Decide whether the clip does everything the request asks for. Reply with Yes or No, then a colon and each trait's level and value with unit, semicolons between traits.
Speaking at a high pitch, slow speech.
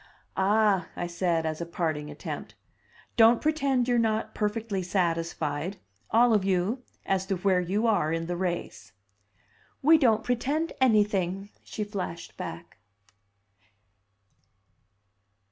Yes: high, 195 Hz; slow, 120 wpm